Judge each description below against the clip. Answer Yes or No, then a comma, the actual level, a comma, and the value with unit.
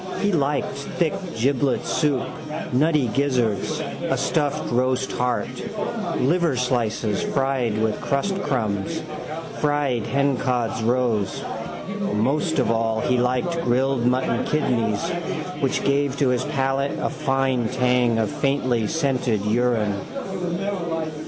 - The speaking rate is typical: No, slow, 105 wpm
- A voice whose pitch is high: No, low, 130 Hz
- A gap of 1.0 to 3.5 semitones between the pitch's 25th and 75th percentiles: Yes, average, 3.1 semitones